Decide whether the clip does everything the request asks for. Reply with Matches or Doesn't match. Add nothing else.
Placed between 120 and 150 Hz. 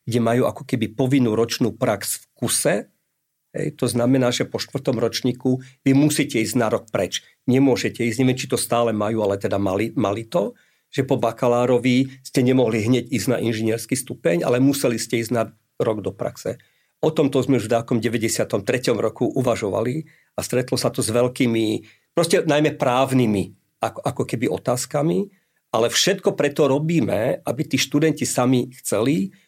Matches